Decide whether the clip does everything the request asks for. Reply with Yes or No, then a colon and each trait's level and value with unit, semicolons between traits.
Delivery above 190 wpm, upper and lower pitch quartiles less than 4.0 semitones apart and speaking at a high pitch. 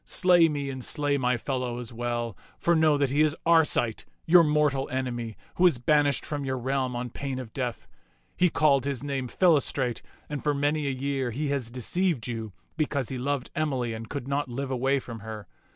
No: average, 200 wpm; average, 3.2 semitones; low, 135 Hz